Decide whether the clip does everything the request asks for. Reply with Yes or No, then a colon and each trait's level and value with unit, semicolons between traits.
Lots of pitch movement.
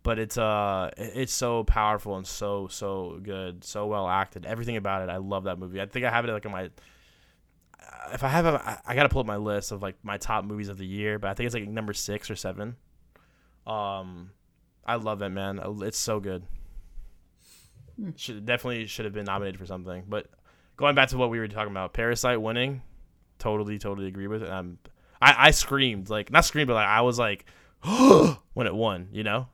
No: average, 3.5 semitones